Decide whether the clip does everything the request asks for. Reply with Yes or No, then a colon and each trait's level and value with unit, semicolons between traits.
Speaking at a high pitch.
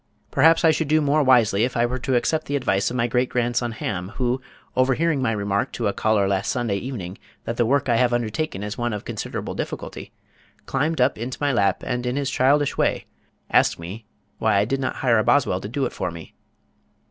No: low, 120 Hz